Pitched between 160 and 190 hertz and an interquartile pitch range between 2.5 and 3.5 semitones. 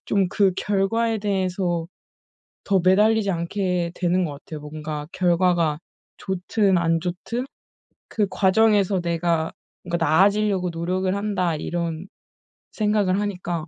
Yes: medium, 185 Hz; average, 2.9 semitones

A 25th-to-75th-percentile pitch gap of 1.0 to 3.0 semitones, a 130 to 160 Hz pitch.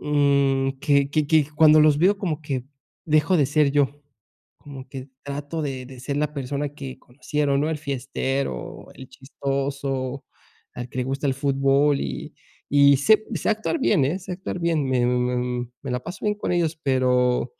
Yes: narrow, 2.4 semitones; medium, 140 Hz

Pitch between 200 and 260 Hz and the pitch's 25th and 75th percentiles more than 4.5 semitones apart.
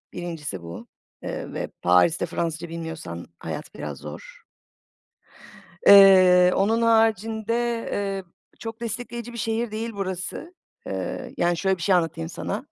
No: high, 190 Hz; average, 5.1 semitones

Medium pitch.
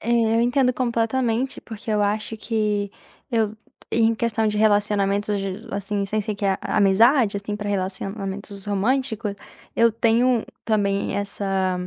No: high, 210 Hz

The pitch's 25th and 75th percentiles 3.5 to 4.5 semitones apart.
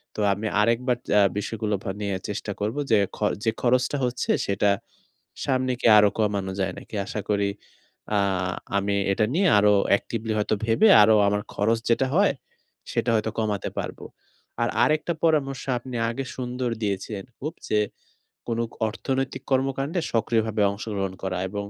Yes: average, 3.9 semitones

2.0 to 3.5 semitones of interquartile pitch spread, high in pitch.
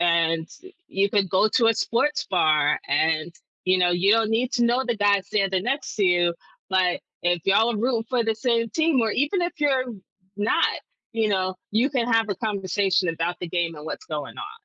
No: average, 4.9 semitones; high, 205 Hz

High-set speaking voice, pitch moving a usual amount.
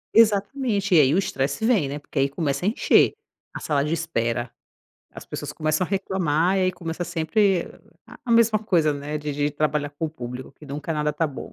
No: medium, 160 Hz; average, 4.7 semitones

